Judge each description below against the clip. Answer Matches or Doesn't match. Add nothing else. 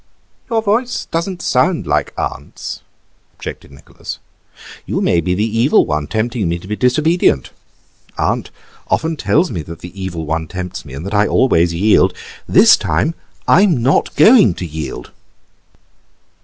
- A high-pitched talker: Doesn't match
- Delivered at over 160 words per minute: Doesn't match